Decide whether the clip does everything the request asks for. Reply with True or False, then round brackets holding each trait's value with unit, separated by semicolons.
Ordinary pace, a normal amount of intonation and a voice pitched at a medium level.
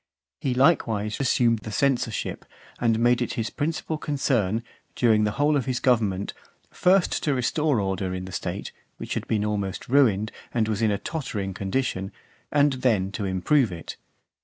False (165 wpm; 4.9 semitones; 115 Hz)